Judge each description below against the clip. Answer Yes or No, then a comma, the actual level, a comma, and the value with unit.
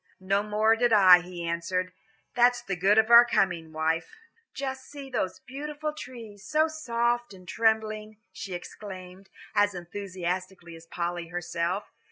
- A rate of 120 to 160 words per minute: Yes, average, 150 wpm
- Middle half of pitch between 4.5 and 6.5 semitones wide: Yes, average, 5.0 semitones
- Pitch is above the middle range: Yes, high, 200 Hz